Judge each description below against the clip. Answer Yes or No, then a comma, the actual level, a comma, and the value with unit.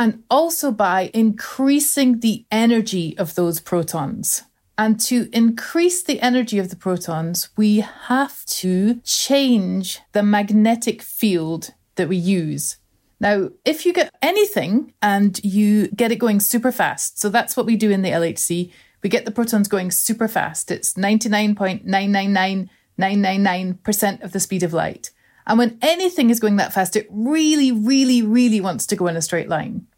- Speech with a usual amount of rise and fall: Yes, average, 3.8 semitones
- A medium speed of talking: Yes, average, 160 wpm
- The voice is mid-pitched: No, high, 210 Hz